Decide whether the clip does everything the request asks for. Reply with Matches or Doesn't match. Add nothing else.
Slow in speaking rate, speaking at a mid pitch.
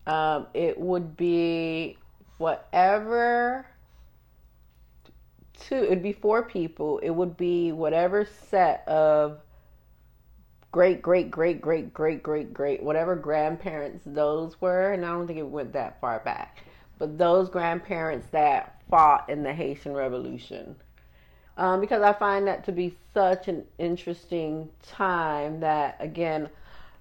Matches